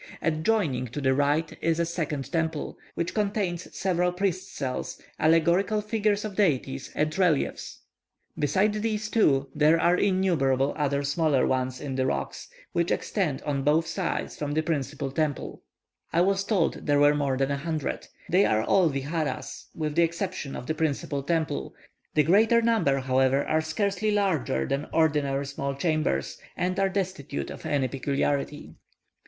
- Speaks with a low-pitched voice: No, medium, 155 Hz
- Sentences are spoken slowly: No, average, 160 wpm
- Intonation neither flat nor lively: Yes, average, 4.9 semitones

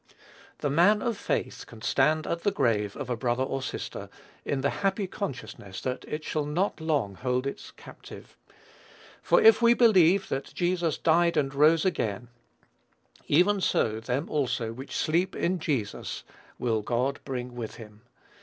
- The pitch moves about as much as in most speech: No, wide, 6.2 semitones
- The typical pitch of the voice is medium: Yes, medium, 145 Hz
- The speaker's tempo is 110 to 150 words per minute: No, average, 160 wpm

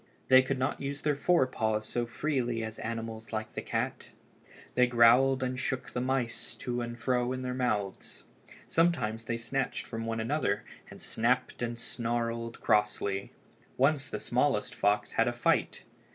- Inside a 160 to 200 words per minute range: Yes, average, 165 wpm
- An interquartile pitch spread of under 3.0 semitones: Yes, narrow, 2.4 semitones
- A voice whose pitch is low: Yes, low, 120 Hz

